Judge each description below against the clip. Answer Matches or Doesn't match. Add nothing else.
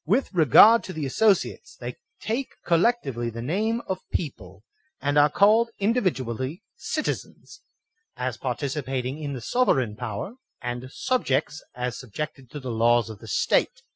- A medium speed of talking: Matches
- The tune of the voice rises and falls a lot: Matches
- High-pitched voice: Doesn't match